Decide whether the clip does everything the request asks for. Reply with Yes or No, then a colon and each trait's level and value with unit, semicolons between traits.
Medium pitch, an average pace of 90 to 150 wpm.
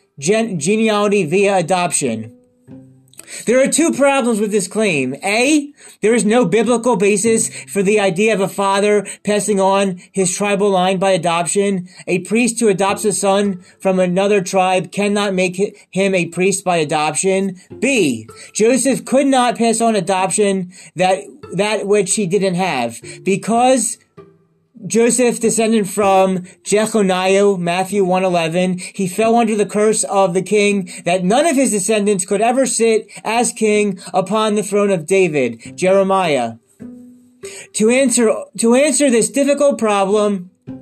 No: high, 200 Hz; average, 145 wpm